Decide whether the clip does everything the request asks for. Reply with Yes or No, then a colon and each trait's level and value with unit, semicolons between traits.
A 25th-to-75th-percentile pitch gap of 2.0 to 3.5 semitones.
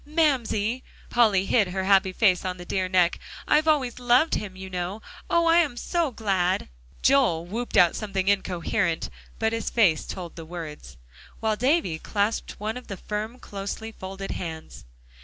No: average, 4.8 semitones